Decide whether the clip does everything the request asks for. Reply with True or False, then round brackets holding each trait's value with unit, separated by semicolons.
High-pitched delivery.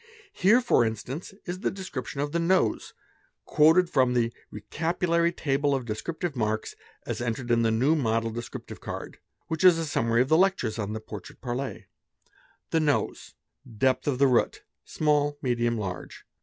False (135 Hz)